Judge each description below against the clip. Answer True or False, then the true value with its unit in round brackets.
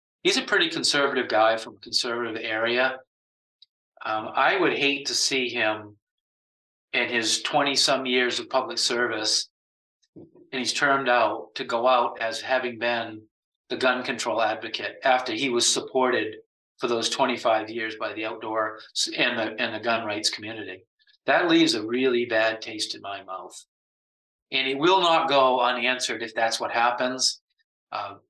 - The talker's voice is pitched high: False (120 Hz)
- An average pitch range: True (3.4 semitones)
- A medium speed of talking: True (160 wpm)